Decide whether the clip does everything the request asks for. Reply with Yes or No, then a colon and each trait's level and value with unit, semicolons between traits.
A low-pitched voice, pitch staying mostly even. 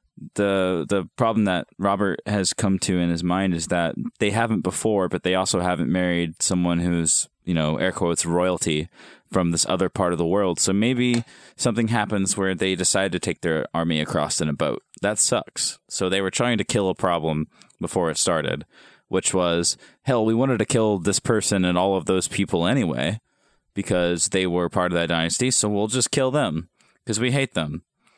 No: very low, 95 Hz; average, 3.2 semitones